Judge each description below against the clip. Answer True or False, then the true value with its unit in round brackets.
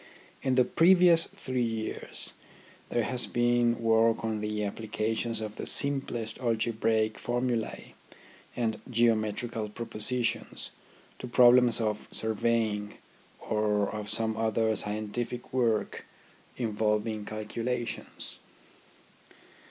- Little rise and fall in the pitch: True (2.0 semitones)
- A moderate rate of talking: False (100 wpm)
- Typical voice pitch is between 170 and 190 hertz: False (115 Hz)